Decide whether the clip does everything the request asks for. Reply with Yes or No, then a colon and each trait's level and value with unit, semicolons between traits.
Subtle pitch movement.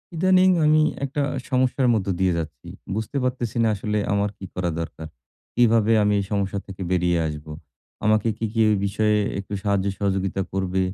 No: average, 3.3 semitones